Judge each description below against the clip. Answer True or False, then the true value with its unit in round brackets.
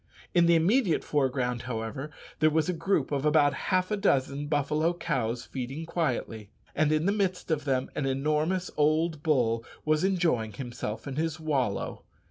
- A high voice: False (150 Hz)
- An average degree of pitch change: True (4.0 semitones)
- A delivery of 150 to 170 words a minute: True (165 wpm)